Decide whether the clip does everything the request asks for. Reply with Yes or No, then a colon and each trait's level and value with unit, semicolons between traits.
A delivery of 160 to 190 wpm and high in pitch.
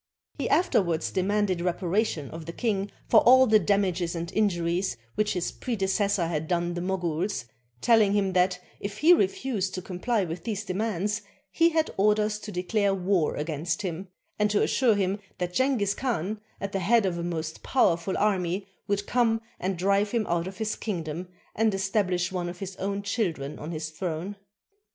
Yes: average, 180 wpm; high, 195 Hz